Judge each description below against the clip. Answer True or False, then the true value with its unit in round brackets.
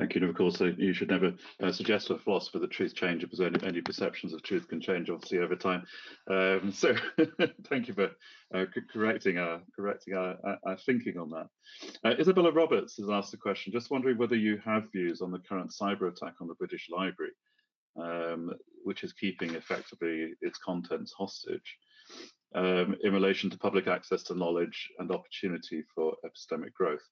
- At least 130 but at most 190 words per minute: True (185 wpm)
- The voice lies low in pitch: True (100 Hz)